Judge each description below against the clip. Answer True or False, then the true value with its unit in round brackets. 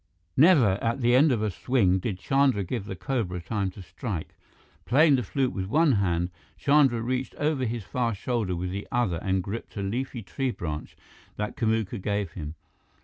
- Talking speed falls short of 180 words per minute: False (185 wpm)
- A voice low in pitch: True (110 Hz)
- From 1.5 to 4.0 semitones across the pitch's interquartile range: False (5.3 semitones)